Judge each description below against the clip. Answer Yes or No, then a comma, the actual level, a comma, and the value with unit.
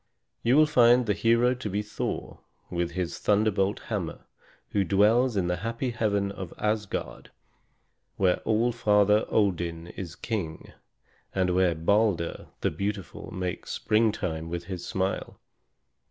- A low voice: Yes, low, 100 Hz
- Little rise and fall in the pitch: No, average, 3.7 semitones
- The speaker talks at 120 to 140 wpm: Yes, slow, 135 wpm